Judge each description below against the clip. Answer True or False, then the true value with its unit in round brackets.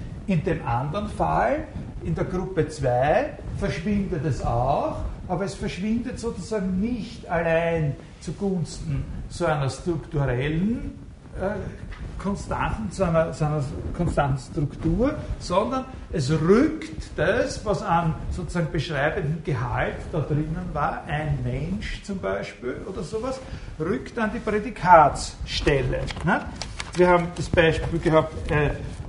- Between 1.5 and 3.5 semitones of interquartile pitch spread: False (4.8 semitones)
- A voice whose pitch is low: False (165 Hz)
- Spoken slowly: True (120 wpm)